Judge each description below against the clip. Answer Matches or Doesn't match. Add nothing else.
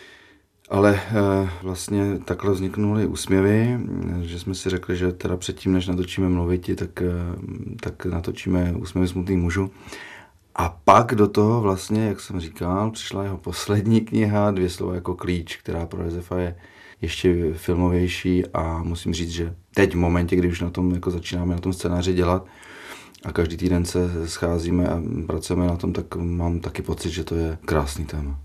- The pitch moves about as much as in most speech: Doesn't match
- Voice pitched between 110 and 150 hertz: Doesn't match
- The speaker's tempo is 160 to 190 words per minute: Matches